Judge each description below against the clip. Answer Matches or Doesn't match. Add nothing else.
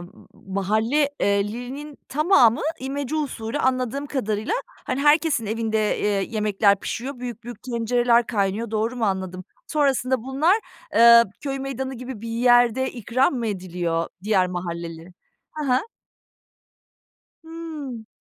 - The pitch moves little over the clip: Doesn't match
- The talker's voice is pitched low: Doesn't match